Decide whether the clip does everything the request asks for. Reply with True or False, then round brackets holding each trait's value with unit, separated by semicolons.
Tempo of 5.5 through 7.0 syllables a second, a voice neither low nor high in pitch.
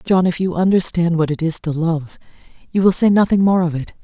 True (5.7 syllables/s; 175 Hz)